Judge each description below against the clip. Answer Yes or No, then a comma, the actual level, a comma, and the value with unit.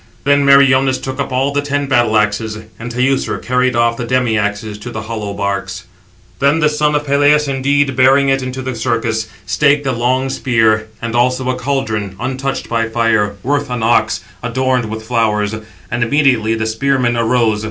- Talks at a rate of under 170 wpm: No, average, 180 wpm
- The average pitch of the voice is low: Yes, low, 125 Hz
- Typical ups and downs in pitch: Yes, average, 3.3 semitones